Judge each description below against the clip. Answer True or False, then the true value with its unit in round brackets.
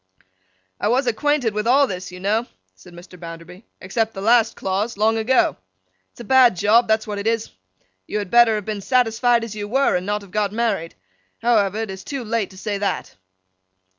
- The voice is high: True (215 Hz)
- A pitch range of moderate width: True (3.1 semitones)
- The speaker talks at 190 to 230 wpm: True (195 wpm)